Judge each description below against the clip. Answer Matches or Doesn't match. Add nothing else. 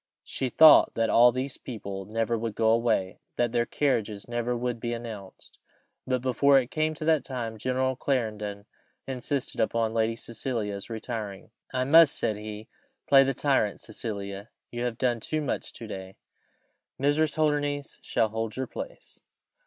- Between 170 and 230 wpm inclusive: Doesn't match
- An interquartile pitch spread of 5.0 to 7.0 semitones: Doesn't match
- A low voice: Matches